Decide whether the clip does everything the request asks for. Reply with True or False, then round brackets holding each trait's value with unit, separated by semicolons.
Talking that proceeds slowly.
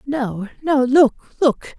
True (100 wpm)